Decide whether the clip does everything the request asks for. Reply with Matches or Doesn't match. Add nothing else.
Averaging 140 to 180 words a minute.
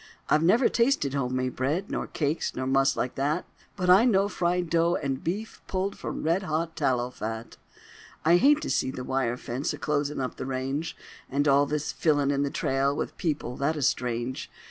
Doesn't match